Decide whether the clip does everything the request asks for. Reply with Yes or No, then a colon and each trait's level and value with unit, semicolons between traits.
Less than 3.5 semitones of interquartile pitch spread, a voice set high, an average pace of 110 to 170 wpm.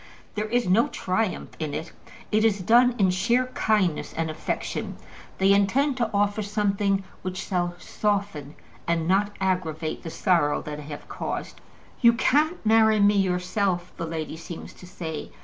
No: average, 3.9 semitones; high, 195 Hz; average, 160 wpm